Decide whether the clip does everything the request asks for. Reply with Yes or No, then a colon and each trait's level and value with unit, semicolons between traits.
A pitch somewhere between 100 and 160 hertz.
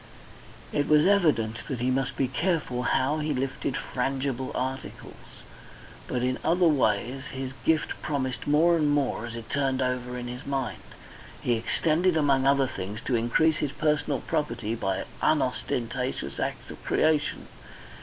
Yes: low, 135 Hz